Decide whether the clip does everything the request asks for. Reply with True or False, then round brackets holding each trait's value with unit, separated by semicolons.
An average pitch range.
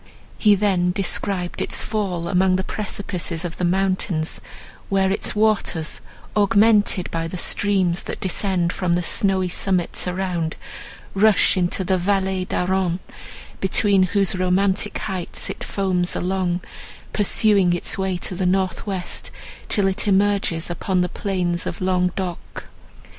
False (1.8 semitones)